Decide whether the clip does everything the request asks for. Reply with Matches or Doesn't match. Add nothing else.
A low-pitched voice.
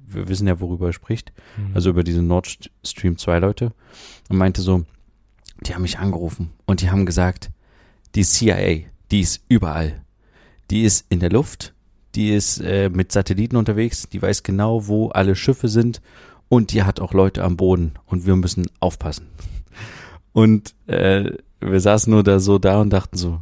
Matches